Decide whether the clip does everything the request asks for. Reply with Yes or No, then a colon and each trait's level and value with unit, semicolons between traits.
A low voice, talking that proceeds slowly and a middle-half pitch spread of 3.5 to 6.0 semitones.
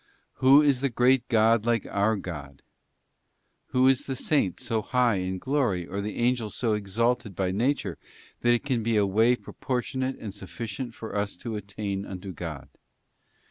No: low, 110 Hz; average, 170 wpm; average, 4.1 semitones